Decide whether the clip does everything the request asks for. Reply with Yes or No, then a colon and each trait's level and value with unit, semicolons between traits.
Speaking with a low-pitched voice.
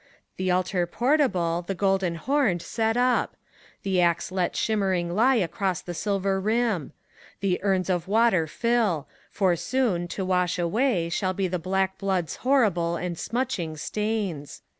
No: high, 190 Hz